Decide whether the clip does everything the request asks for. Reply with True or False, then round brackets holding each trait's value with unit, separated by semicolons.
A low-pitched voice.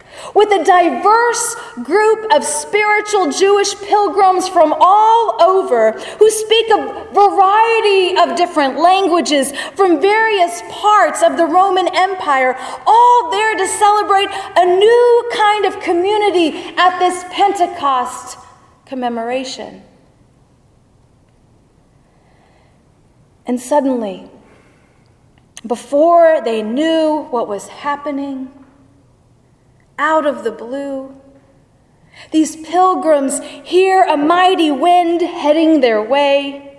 False (345 Hz)